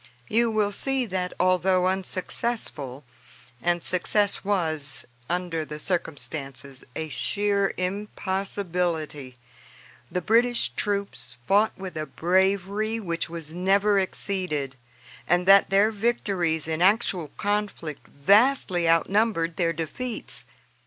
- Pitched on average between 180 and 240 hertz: Yes, medium, 185 Hz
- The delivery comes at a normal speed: No, slow, 105 wpm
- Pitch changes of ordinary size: Yes, average, 3.9 semitones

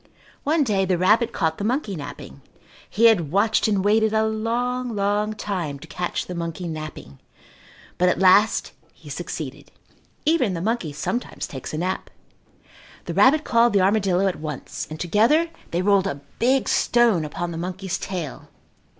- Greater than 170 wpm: No, average, 165 wpm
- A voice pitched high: Yes, high, 195 Hz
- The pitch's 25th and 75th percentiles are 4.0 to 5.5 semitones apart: Yes, average, 4.6 semitones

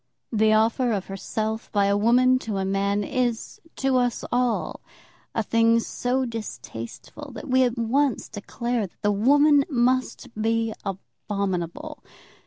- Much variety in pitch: No, average, 3.7 semitones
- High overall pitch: Yes, high, 230 Hz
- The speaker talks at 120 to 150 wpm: Yes, average, 140 wpm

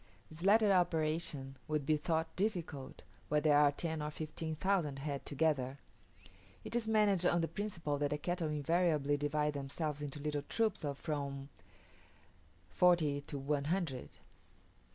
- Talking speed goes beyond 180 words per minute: No, average, 150 wpm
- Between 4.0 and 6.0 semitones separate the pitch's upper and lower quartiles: No, average, 3.2 semitones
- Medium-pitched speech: Yes, medium, 155 Hz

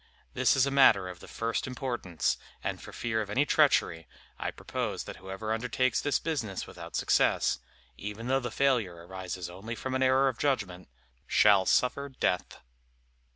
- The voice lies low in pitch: Yes, low, 115 Hz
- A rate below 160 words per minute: No, average, 165 wpm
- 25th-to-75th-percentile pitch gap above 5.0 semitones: Yes, wide, 5.6 semitones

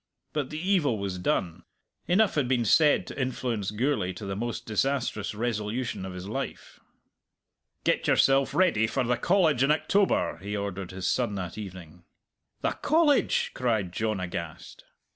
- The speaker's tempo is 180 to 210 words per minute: No, average, 155 wpm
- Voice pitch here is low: Yes, low, 115 Hz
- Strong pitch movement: Yes, wide, 6.1 semitones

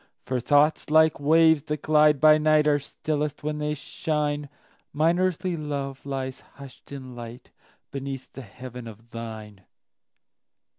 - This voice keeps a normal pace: No, slow, 120 wpm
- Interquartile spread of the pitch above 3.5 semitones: No, average, 2.8 semitones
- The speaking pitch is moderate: Yes, medium, 145 Hz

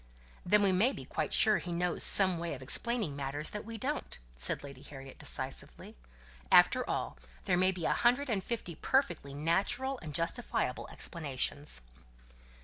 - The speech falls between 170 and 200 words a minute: No, average, 160 wpm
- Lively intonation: Yes, wide, 7.4 semitones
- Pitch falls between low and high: Yes, medium, 180 Hz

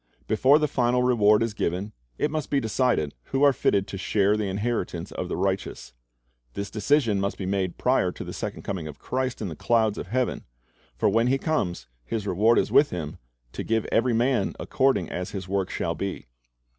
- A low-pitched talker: Yes, low, 105 Hz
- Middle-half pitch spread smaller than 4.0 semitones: No, average, 4.6 semitones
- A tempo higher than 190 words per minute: Yes, average, 200 wpm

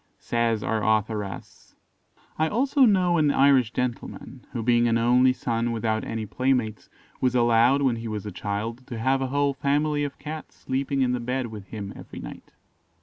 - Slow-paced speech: No, average, 180 wpm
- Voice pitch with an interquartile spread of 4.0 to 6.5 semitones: No, average, 3.5 semitones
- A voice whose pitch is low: Yes, low, 125 Hz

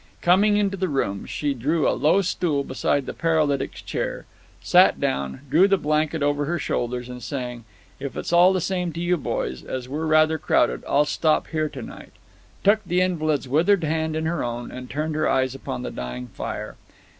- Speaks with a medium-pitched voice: Yes, medium, 155 Hz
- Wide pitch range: No, average, 4.8 semitones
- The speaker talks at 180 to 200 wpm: Yes, average, 190 wpm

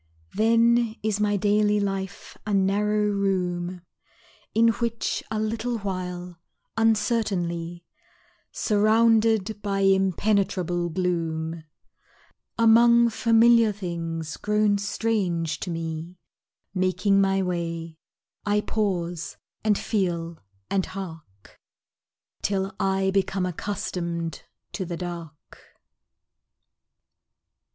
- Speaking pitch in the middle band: No, high, 195 Hz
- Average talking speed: No, slow, 90 wpm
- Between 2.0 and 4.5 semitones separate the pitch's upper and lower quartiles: Yes, average, 3.5 semitones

